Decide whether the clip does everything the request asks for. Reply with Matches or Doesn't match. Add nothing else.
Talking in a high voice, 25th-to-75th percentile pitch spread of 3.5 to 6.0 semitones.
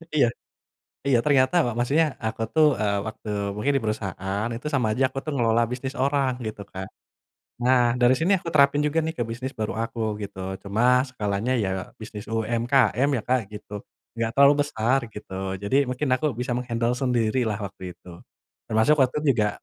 Doesn't match